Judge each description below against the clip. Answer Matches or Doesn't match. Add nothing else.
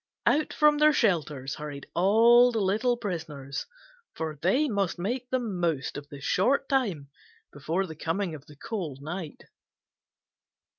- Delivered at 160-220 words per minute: Doesn't match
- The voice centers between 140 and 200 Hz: Matches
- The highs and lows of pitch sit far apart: Matches